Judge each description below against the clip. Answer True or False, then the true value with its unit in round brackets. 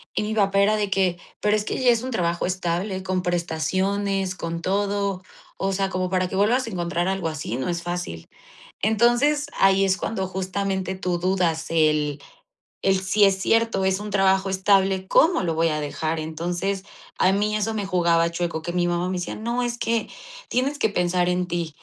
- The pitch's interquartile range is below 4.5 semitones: True (2.7 semitones)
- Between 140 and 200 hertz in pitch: True (190 Hz)